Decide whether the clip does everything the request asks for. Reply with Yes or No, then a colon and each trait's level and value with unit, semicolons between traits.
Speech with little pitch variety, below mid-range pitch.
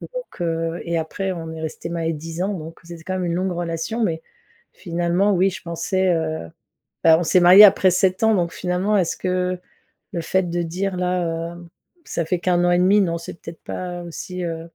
No: narrow, 1.9 semitones; medium, 175 Hz